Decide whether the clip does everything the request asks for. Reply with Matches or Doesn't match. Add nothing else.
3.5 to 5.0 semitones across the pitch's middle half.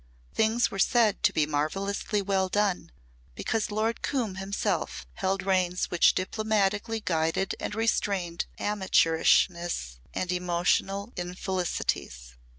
Doesn't match